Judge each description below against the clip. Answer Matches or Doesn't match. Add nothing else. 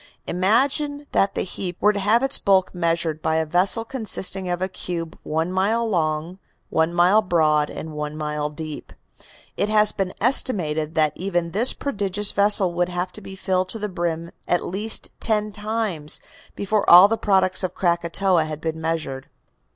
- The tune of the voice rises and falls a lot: Doesn't match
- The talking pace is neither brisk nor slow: Matches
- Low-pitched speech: Doesn't match